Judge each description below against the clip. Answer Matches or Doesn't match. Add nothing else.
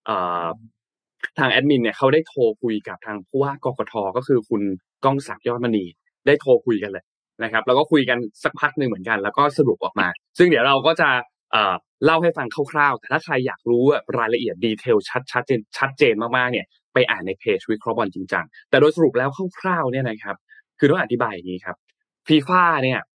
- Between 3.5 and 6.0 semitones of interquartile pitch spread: Matches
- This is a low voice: Matches